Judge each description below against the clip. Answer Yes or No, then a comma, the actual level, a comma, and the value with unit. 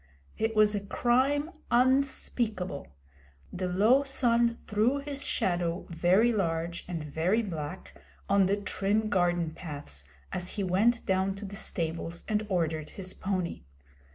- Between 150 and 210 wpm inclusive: No, slow, 135 wpm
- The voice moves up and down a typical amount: Yes, average, 4.9 semitones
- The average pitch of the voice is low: No, high, 195 Hz